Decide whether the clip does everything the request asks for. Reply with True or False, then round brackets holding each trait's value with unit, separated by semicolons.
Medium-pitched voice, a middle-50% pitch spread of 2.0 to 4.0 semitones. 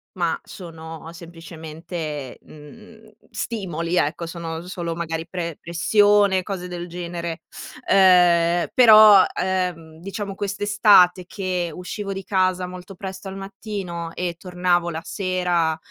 True (180 Hz; 2.5 semitones)